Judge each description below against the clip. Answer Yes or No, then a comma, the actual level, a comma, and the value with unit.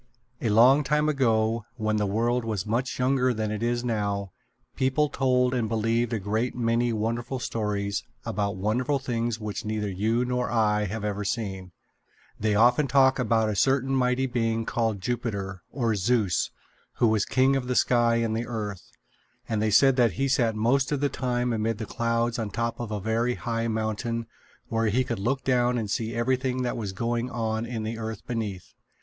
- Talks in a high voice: No, low, 115 Hz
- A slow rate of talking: No, average, 190 wpm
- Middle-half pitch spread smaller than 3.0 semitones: Yes, narrow, 2.4 semitones